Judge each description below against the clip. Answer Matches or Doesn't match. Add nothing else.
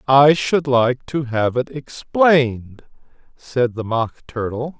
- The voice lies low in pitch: Matches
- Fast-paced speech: Doesn't match